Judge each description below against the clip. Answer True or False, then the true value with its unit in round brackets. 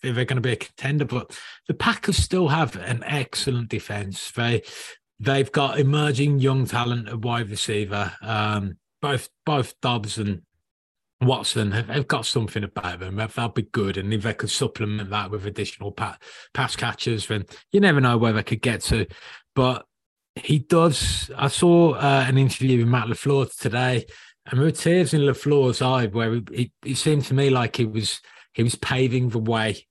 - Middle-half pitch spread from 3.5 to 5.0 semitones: True (4.0 semitones)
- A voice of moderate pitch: False (120 Hz)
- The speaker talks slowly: False (180 wpm)